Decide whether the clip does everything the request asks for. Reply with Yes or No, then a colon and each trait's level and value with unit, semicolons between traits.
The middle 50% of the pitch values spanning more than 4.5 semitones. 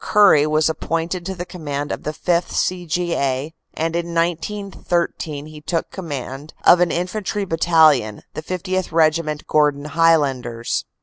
No: average, 2.8 semitones